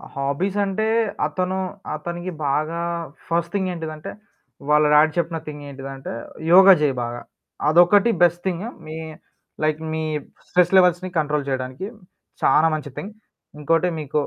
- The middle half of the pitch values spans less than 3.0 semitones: No, average, 3.3 semitones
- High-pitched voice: No, medium, 165 Hz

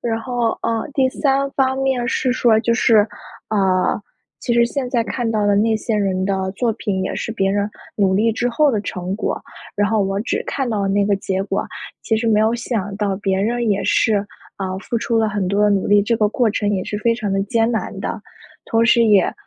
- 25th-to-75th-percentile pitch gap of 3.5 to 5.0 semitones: No, average, 2.9 semitones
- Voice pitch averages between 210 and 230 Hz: Yes, high, 215 Hz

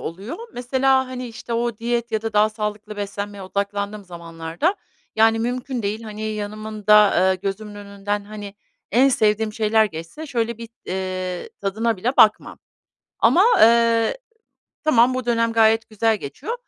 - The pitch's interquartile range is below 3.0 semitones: Yes, narrow, 2.5 semitones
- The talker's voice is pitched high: Yes, high, 215 Hz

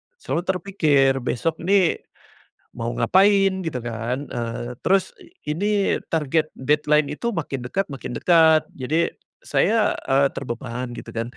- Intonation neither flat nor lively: No, wide, 6.5 semitones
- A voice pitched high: No, medium, 150 Hz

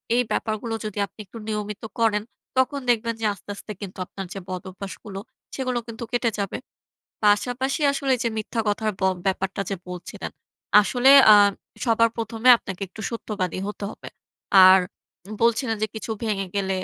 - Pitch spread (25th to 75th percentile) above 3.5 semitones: No, average, 2.8 semitones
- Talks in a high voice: Yes, high, 215 Hz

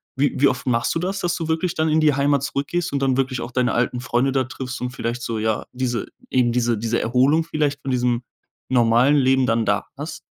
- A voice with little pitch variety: No, average, 3.2 semitones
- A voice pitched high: No, low, 130 Hz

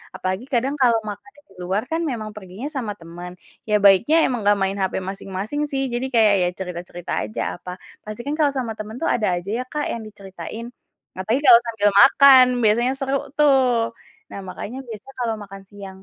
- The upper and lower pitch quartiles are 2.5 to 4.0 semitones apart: No, average, 4.6 semitones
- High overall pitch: Yes, high, 220 Hz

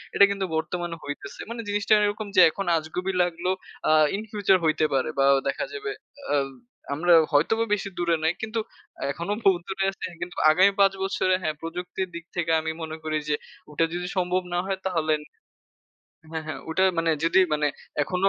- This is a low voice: No, medium, 175 Hz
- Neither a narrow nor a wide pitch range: Yes, average, 3.3 semitones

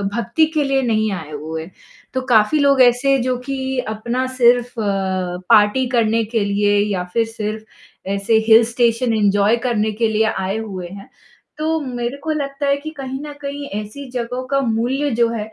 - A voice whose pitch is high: Yes, high, 235 Hz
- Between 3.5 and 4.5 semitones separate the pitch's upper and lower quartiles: Yes, average, 3.8 semitones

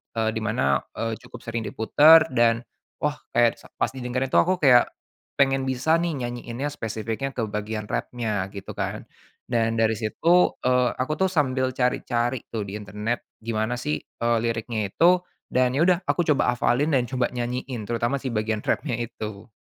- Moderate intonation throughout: Yes, average, 3.0 semitones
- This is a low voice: Yes, low, 120 Hz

